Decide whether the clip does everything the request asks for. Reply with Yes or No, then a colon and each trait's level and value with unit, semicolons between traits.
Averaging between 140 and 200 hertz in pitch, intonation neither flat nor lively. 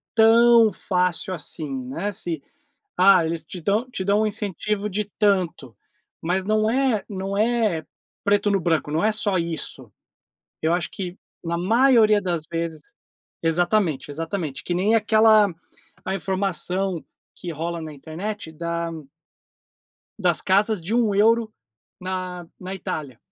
Yes: high, 190 Hz; average, 4.0 semitones